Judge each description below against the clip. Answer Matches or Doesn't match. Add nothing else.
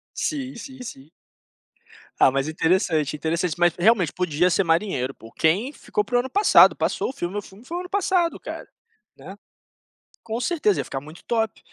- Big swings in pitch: Matches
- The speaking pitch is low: Doesn't match